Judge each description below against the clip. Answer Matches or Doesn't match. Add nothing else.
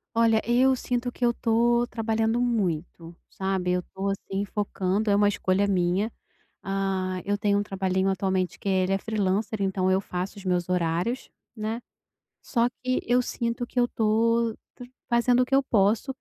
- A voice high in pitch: Matches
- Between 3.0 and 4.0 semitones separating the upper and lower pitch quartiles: Matches